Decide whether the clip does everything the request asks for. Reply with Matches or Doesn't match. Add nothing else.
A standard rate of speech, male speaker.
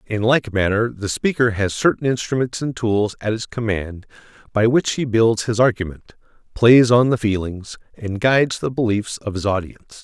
Matches